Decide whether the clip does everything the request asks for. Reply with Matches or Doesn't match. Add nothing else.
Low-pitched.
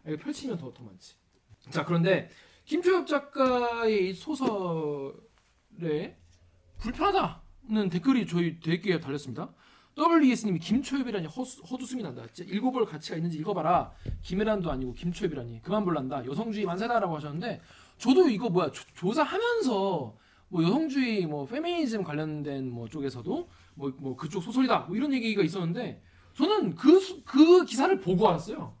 Doesn't match